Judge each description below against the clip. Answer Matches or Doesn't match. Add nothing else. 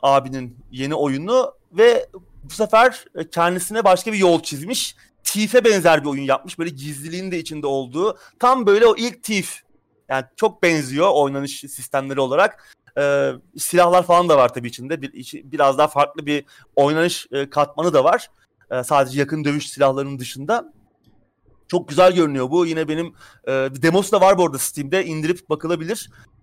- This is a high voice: Doesn't match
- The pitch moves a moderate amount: Matches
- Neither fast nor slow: Doesn't match